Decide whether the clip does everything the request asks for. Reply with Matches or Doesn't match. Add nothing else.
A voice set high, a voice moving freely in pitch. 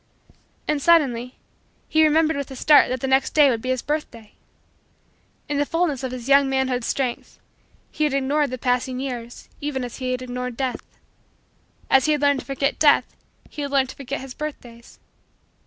Doesn't match